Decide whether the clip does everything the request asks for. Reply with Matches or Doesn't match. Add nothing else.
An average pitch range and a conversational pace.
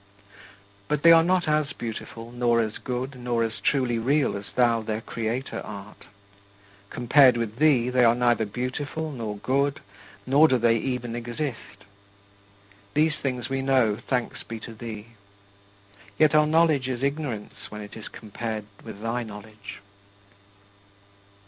Matches